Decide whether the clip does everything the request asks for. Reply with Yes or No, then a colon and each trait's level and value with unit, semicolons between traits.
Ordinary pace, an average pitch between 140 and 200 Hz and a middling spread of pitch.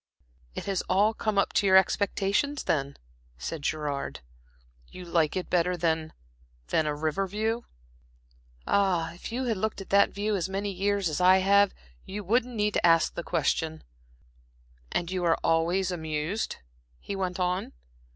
Yes: average, 160 wpm; medium, 185 Hz; average, 3.6 semitones